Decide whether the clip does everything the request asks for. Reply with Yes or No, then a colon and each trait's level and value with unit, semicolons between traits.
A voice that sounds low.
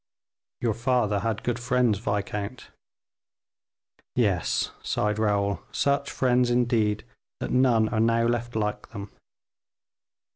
Yes: low, 115 Hz